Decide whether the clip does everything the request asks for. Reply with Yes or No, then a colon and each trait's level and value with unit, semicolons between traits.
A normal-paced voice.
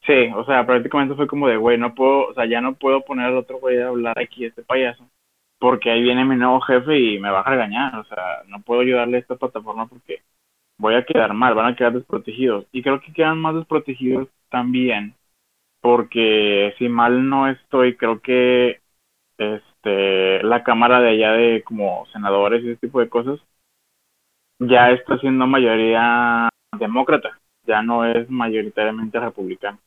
Yes: average, 180 wpm